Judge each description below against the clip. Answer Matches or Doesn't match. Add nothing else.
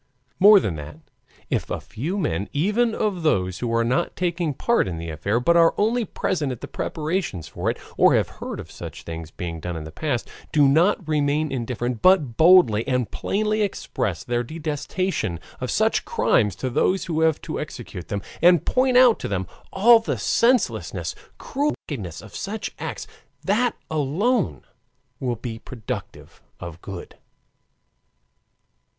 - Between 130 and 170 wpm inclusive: Matches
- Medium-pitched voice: Matches